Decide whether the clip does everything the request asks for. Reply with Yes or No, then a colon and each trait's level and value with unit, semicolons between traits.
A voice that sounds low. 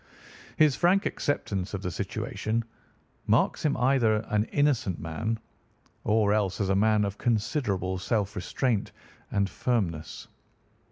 Yes: low, 105 Hz